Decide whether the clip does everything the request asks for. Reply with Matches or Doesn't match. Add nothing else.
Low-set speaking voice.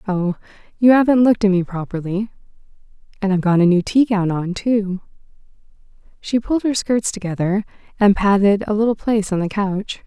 Doesn't match